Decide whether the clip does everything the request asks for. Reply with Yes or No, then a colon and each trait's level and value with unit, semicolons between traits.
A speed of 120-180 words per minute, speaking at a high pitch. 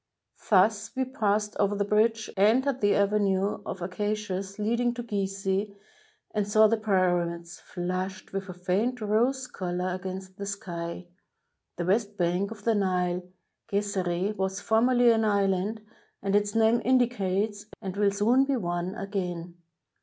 Yes: average, 145 wpm; high, 200 Hz